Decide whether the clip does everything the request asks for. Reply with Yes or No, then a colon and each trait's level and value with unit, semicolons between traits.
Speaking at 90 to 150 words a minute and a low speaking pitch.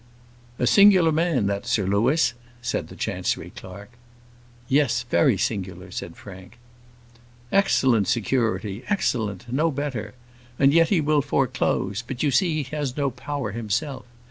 Yes: average, 140 wpm; low, 125 Hz